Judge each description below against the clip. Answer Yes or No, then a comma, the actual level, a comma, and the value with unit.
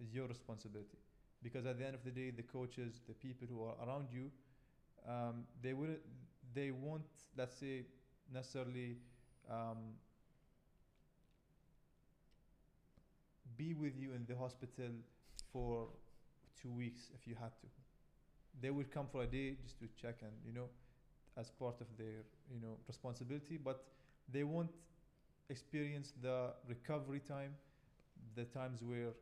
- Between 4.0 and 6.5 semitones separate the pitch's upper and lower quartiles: No, narrow, 2.6 semitones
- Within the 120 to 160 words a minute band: Yes, average, 140 wpm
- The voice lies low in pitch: Yes, low, 130 Hz